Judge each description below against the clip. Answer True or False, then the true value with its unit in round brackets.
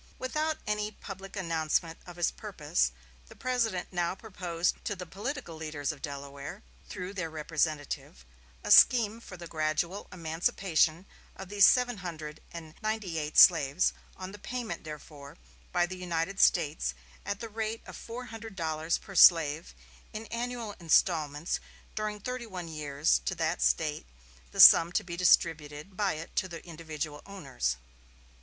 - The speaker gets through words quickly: False (150 wpm)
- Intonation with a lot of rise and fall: False (4.8 semitones)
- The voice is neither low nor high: True (175 Hz)